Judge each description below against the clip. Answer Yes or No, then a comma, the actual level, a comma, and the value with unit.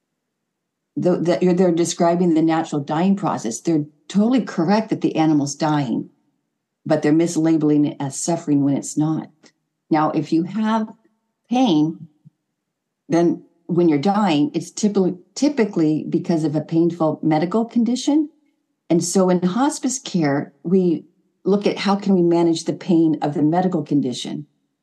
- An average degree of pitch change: Yes, average, 3.9 semitones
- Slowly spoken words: No, average, 145 wpm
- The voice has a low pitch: No, medium, 170 Hz